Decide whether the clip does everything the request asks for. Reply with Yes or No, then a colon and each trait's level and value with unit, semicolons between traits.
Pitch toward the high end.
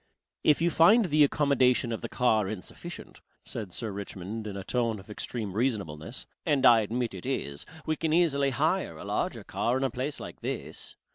No: low, 120 Hz